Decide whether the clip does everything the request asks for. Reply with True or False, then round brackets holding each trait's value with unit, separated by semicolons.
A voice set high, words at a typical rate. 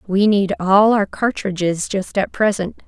True (195 Hz; 165 wpm)